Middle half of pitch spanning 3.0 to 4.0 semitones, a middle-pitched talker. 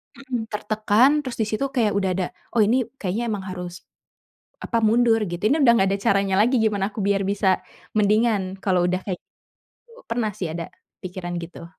No: average, 3.4 semitones; high, 205 Hz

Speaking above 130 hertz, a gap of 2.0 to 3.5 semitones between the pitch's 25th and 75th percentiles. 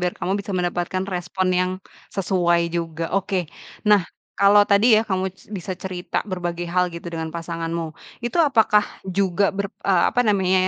Yes: medium, 185 Hz; narrow, 2.4 semitones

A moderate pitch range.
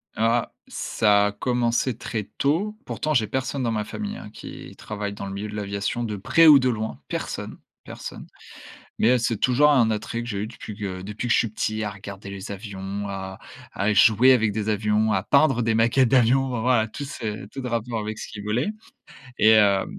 Yes: average, 3.0 semitones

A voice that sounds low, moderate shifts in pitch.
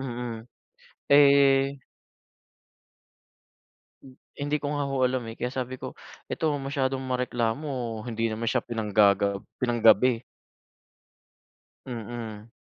Yes: low, 125 Hz; average, 3.0 semitones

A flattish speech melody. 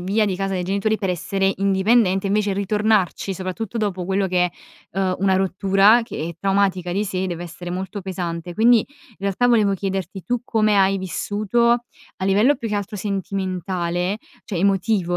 Yes: narrow, 2.1 semitones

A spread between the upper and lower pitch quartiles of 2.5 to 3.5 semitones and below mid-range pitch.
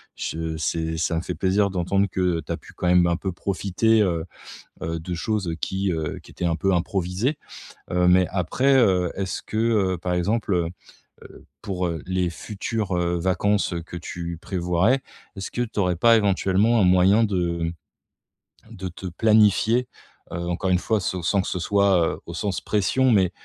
Yes: average, 2.8 semitones; very low, 95 Hz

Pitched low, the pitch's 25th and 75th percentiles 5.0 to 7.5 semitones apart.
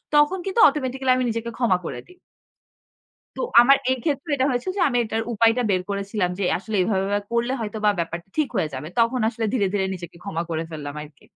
No: high, 225 Hz; wide, 5.5 semitones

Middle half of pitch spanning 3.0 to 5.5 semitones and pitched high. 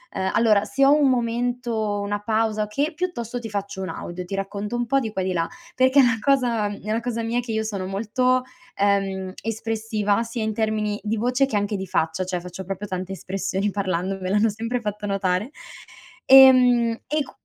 Yes: average, 3.4 semitones; high, 215 Hz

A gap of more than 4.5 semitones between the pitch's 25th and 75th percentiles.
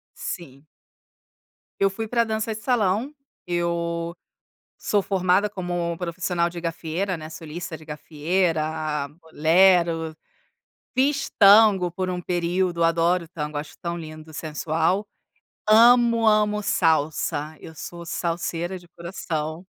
No: average, 3.0 semitones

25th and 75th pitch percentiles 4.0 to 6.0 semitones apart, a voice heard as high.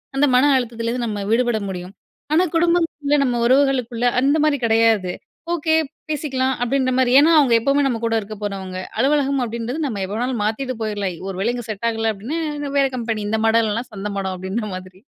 Yes: average, 4.3 semitones; high, 235 Hz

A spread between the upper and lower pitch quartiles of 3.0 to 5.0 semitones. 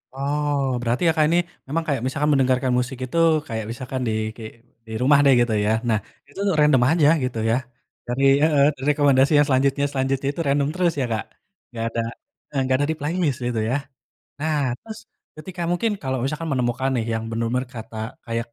Yes: average, 3.3 semitones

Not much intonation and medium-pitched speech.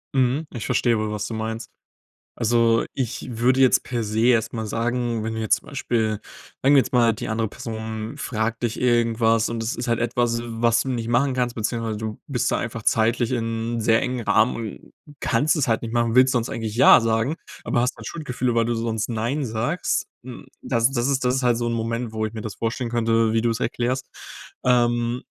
No: narrow, 1.6 semitones; low, 115 Hz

